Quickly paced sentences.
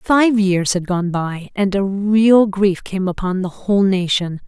No: average, 190 wpm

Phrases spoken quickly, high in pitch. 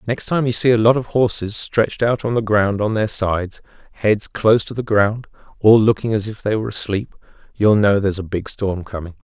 No: fast, 225 wpm; low, 105 Hz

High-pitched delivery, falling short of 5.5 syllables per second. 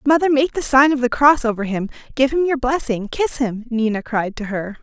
Yes: very high, 255 Hz; 5.3 syllables/s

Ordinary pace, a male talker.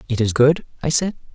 No: fast, 225 wpm; male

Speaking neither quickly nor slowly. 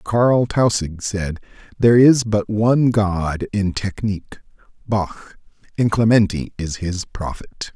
No: slow, 125 wpm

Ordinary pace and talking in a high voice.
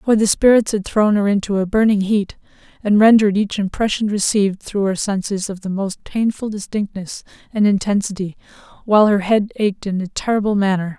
Yes: average, 180 wpm; high, 205 Hz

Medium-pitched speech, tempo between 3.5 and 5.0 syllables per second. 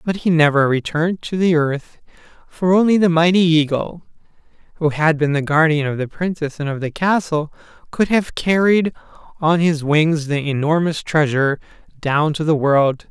Yes: medium, 160 Hz; 4.8 syllables/s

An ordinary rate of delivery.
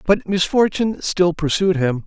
Yes: average, 145 wpm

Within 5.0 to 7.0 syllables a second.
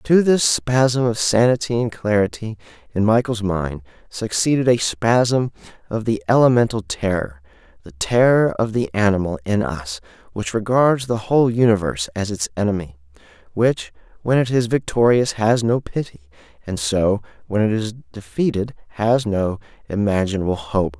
No: 4.7 syllables/s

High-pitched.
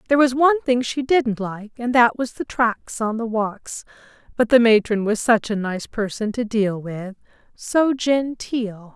Yes: high, 230 Hz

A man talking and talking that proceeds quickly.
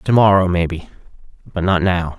No: male; slow, 135 wpm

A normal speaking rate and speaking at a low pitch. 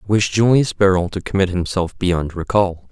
Yes: average, 185 wpm; very low, 95 Hz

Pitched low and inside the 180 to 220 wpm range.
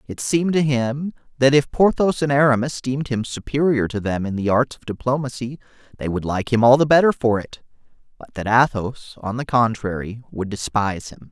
Yes: low, 125 Hz; average, 195 wpm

